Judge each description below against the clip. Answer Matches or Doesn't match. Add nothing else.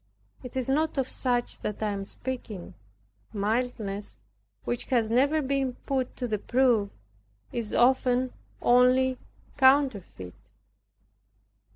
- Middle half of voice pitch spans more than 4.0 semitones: Doesn't match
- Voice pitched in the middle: Doesn't match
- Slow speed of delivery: Matches